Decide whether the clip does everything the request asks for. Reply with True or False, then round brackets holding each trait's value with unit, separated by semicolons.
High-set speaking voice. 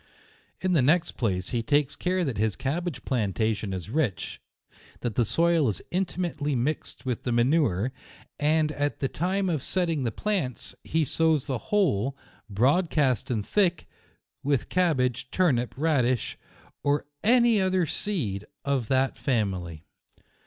False (140 Hz)